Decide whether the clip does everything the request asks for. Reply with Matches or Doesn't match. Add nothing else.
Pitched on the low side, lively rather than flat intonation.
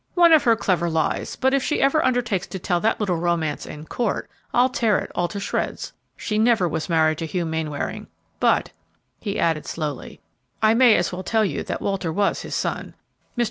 Doesn't match